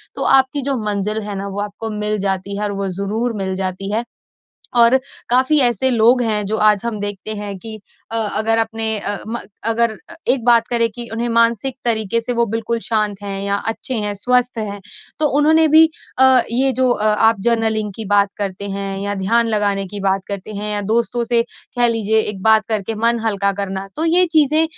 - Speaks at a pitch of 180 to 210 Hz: No, high, 220 Hz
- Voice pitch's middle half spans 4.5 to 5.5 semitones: No, average, 2.7 semitones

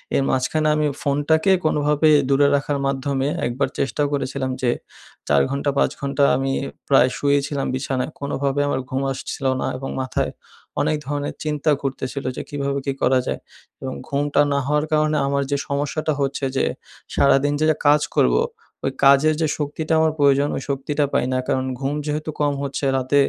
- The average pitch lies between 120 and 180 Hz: Yes, medium, 140 Hz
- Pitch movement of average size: No, narrow, 1.5 semitones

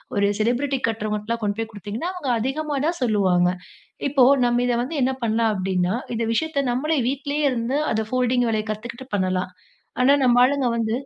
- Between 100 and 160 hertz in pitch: No, high, 235 Hz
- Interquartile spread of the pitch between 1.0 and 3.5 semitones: No, average, 4.0 semitones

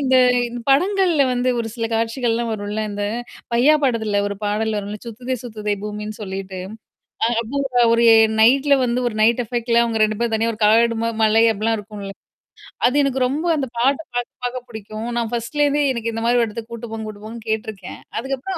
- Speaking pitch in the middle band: No, high, 230 Hz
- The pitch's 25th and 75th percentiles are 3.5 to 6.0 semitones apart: No, average, 2.7 semitones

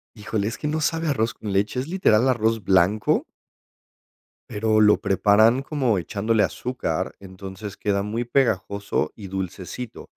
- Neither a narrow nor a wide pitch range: Yes, average, 3.5 semitones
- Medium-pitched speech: No, low, 110 Hz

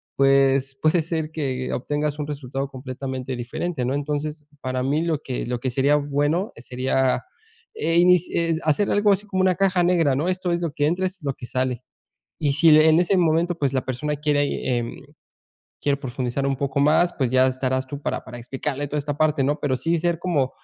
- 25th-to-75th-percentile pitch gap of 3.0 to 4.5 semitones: Yes, average, 3.9 semitones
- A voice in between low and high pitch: Yes, medium, 145 Hz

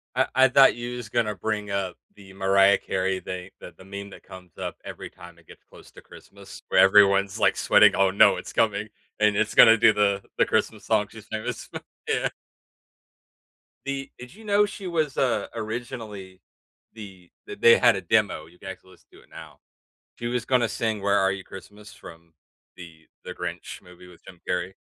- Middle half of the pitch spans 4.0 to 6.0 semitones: No, average, 3.3 semitones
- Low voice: Yes, low, 100 Hz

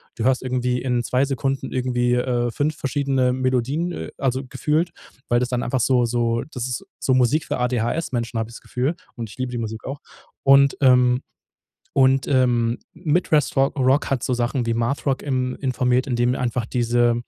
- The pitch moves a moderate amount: No, narrow, 1.9 semitones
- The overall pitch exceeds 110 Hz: Yes, low, 125 Hz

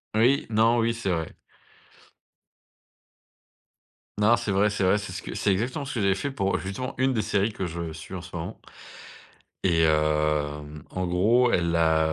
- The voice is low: Yes, very low, 95 Hz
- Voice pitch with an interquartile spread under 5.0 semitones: No, wide, 5.5 semitones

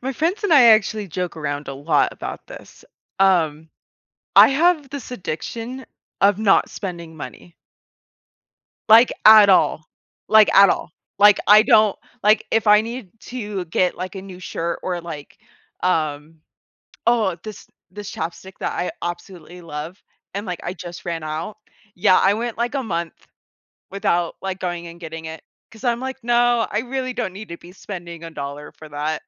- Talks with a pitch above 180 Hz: Yes, high, 190 Hz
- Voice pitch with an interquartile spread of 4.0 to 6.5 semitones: Yes, average, 4.7 semitones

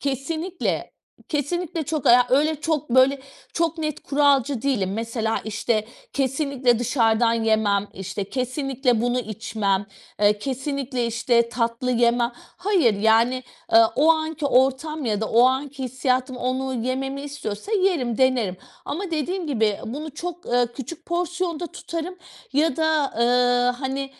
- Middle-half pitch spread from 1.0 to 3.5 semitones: No, average, 4.4 semitones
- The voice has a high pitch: Yes, very high, 260 Hz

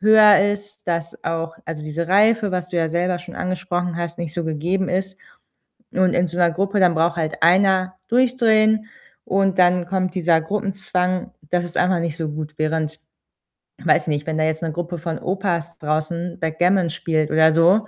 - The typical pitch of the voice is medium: Yes, medium, 175 Hz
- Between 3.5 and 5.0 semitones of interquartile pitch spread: No, average, 2.7 semitones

